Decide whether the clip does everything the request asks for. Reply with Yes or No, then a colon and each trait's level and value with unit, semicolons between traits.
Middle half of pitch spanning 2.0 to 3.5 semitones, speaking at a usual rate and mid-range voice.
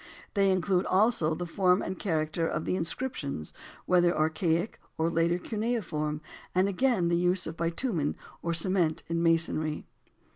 Yes: average, 2.8 semitones; average, 145 wpm; medium, 170 Hz